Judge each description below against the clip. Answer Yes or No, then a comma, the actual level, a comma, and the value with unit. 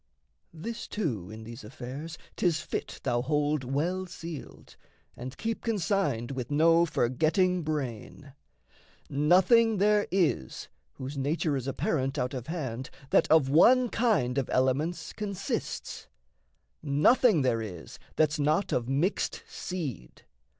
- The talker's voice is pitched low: No, medium, 150 Hz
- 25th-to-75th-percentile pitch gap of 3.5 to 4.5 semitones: No, wide, 5.6 semitones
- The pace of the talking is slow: Yes, slow, 125 wpm